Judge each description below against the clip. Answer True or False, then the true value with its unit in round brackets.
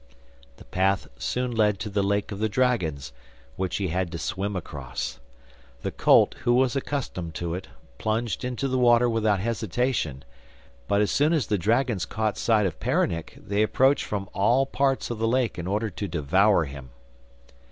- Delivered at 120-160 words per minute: False (175 wpm)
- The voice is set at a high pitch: False (105 Hz)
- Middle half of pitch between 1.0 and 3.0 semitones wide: False (4.8 semitones)